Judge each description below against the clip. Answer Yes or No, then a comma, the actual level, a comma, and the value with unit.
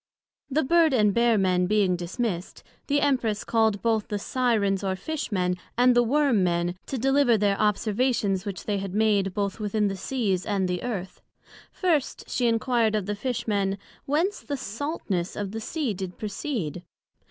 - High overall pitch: Yes, high, 215 Hz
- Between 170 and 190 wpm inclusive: Yes, average, 175 wpm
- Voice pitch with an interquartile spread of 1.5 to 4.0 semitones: No, average, 4.4 semitones